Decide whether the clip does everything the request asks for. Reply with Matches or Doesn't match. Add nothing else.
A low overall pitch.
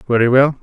Matches